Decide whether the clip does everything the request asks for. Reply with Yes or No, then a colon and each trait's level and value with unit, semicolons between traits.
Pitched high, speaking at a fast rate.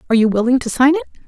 Yes: very high, 250 Hz; fast, 285 wpm